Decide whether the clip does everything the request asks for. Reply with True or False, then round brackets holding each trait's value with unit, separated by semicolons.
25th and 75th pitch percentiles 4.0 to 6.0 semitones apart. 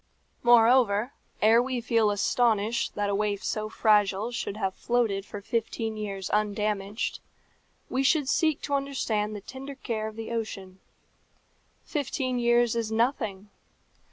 False (2.8 semitones)